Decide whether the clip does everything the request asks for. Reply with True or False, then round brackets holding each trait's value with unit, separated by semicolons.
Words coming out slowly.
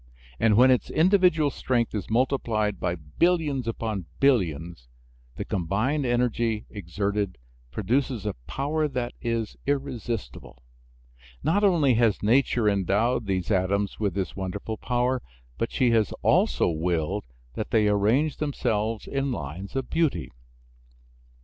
True (125 wpm)